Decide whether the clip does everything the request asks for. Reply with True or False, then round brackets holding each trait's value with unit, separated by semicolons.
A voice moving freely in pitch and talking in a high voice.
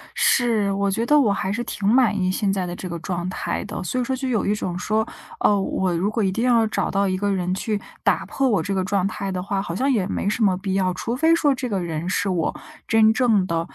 False (3.5 semitones; 200 Hz)